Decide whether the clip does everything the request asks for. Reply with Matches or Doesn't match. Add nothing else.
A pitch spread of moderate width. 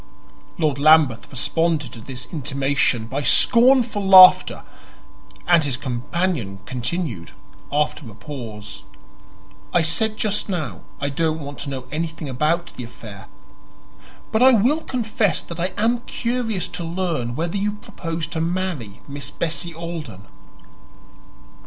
Doesn't match